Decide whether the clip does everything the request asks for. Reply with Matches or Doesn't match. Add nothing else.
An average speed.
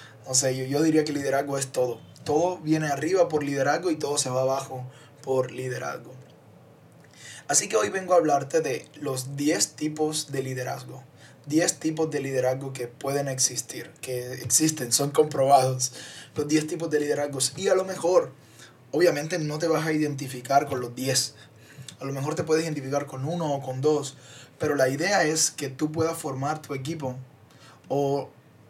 Matches